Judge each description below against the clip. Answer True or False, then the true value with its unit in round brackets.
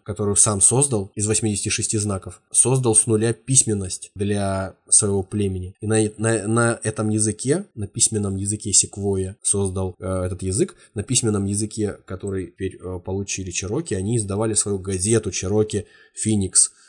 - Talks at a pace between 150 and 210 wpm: False (140 wpm)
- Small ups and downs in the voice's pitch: True (2.1 semitones)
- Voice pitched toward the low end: True (105 Hz)